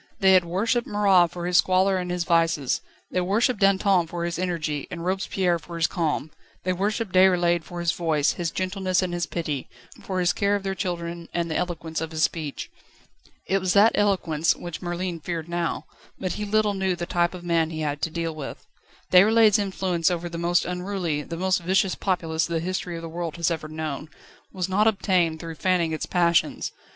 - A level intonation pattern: Yes, narrow, 2.2 semitones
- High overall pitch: No, medium, 175 Hz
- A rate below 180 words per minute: No, average, 200 wpm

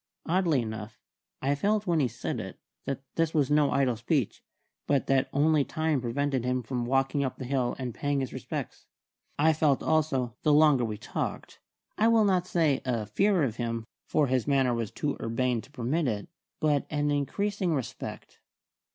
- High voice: No, medium, 140 Hz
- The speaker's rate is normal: Yes, average, 180 wpm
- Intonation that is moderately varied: Yes, average, 4.0 semitones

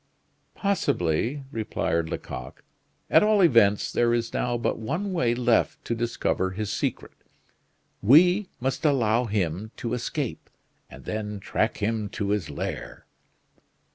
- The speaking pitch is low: Yes, low, 115 Hz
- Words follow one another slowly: Yes, slow, 130 wpm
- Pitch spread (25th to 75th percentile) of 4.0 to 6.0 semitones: Yes, average, 4.3 semitones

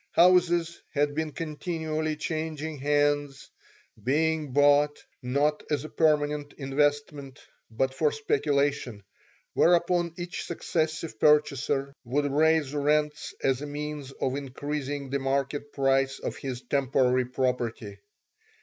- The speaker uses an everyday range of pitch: No, narrow, 2.2 semitones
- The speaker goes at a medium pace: No, slow, 115 wpm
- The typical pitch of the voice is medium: Yes, medium, 145 Hz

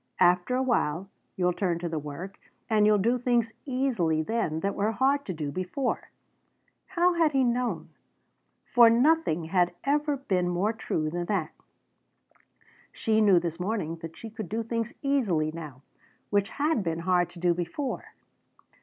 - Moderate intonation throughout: No, wide, 6.1 semitones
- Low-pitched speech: No, high, 200 Hz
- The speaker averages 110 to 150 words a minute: No, average, 165 wpm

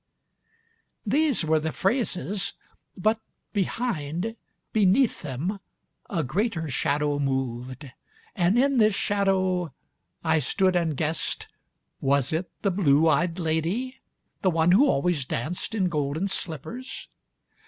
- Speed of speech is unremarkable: No, slow, 120 wpm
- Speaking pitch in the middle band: Yes, medium, 175 Hz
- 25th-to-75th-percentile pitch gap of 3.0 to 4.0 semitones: No, wide, 5.5 semitones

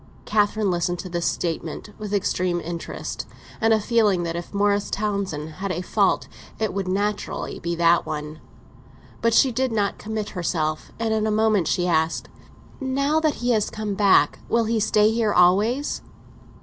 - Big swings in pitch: No, average, 4.0 semitones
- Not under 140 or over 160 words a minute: No, average, 170 wpm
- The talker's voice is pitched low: No, high, 205 Hz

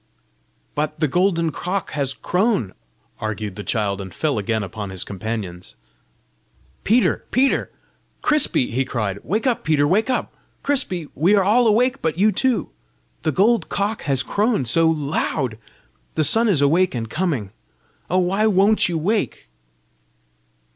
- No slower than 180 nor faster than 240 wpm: No, average, 145 wpm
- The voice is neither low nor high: Yes, medium, 165 Hz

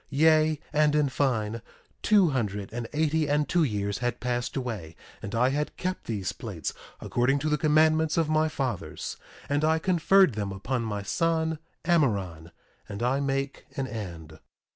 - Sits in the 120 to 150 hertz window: Yes, low, 135 Hz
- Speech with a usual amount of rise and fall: No, wide, 6.2 semitones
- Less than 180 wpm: Yes, average, 165 wpm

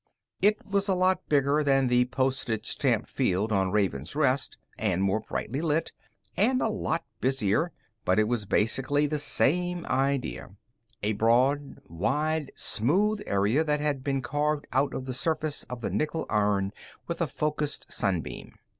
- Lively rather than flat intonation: Yes, wide, 5.9 semitones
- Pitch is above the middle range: No, low, 135 Hz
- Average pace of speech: Yes, average, 160 wpm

